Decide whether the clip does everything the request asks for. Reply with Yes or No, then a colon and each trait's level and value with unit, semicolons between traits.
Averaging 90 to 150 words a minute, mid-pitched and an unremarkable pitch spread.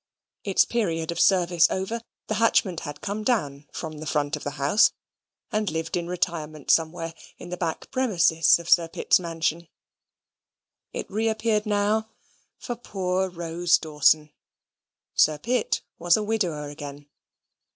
Yes: average, 140 wpm; medium, 170 Hz; average, 4.7 semitones